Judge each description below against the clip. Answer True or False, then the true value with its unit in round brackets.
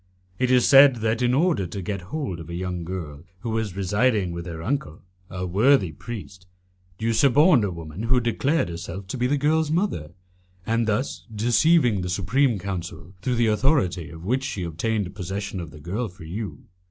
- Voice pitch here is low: True (105 Hz)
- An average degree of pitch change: False (6.0 semitones)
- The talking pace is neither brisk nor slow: True (190 wpm)